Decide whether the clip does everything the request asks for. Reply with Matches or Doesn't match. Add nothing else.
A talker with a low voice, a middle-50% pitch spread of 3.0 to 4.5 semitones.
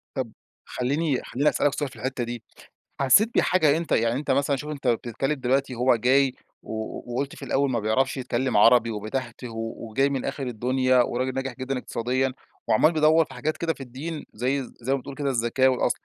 Doesn't match